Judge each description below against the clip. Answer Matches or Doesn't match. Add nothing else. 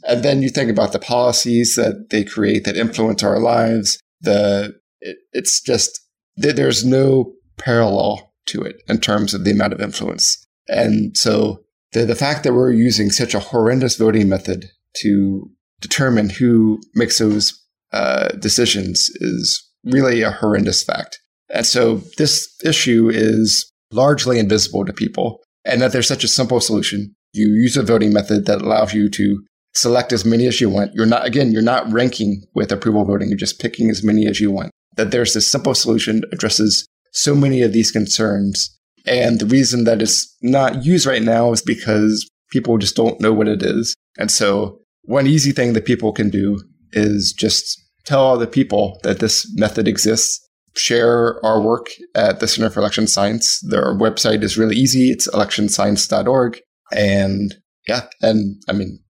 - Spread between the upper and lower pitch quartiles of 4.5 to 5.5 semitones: Doesn't match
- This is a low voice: Matches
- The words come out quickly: Doesn't match